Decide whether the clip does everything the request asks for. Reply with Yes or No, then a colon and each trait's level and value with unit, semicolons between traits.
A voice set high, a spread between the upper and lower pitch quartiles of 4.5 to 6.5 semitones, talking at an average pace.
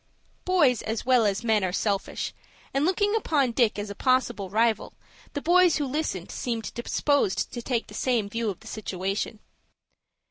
Yes: high, 235 Hz; average, 5.1 semitones; average, 170 wpm